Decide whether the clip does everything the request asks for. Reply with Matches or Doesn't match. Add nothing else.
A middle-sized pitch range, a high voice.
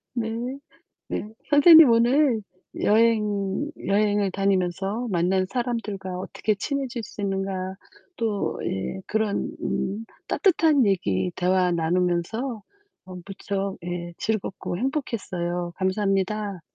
Matches